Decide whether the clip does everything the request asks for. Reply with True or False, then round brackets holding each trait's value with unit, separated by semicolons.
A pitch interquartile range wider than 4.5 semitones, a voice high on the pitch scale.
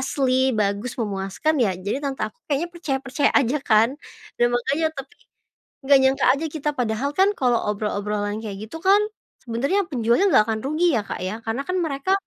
True (5.5 semitones; 265 Hz)